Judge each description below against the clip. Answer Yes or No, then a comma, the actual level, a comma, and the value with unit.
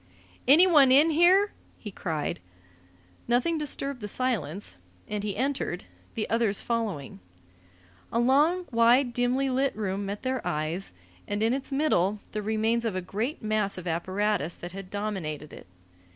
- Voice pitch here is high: Yes, high, 220 Hz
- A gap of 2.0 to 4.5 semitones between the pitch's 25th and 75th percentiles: No, average, 5.2 semitones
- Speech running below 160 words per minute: Yes, average, 150 wpm